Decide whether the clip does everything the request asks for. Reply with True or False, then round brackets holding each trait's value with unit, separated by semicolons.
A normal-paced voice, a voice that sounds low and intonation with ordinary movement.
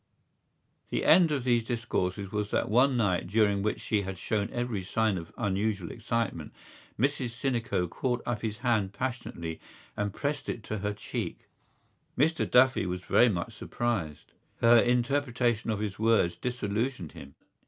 True (155 wpm; 110 Hz; 3.7 semitones)